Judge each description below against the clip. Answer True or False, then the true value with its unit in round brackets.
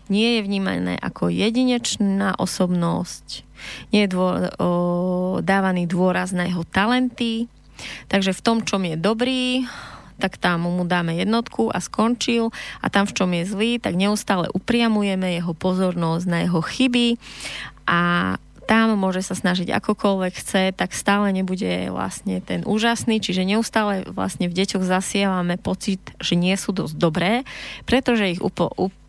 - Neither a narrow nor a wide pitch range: True (3.6 semitones)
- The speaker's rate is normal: True (145 wpm)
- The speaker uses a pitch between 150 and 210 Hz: True (190 Hz)